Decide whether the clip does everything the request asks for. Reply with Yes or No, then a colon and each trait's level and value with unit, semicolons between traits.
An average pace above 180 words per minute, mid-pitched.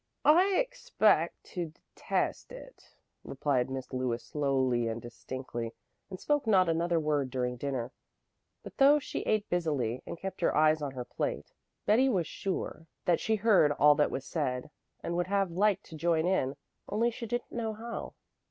No: average, 170 wpm; medium, 165 Hz